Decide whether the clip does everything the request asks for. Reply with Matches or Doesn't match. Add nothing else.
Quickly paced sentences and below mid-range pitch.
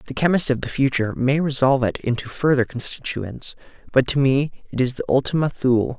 Doesn't match